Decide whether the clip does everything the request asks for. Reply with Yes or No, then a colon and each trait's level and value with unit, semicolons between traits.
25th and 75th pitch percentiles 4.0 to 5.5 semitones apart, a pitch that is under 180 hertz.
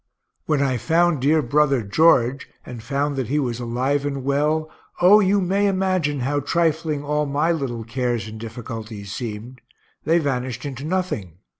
Yes: average, 4.4 semitones; medium, 140 Hz